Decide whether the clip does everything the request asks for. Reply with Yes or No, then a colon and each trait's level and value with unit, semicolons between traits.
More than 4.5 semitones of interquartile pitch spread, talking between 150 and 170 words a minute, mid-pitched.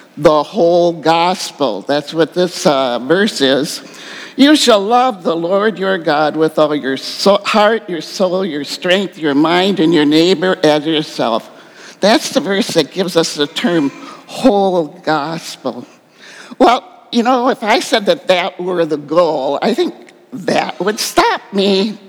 Yes: average, 5.0 semitones; average, 160 wpm; medium, 180 Hz